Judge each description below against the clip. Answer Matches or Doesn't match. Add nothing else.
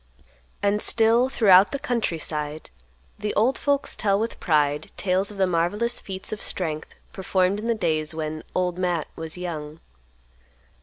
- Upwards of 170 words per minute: Doesn't match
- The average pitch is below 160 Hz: Doesn't match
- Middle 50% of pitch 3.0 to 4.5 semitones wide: Doesn't match